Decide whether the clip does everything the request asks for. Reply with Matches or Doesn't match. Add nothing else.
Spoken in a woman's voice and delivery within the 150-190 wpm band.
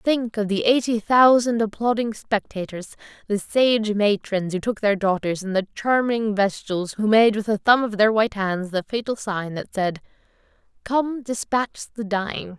Matches